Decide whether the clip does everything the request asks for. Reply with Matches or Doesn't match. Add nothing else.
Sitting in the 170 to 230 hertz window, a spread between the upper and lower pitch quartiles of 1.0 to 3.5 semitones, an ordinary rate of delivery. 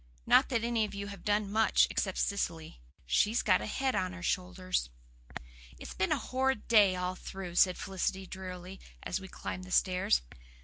Matches